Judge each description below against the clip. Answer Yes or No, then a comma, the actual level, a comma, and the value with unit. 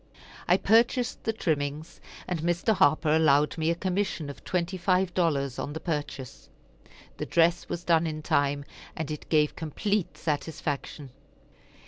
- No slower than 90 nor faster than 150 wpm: Yes, average, 145 wpm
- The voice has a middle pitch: Yes, medium, 160 Hz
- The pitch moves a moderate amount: Yes, average, 3.2 semitones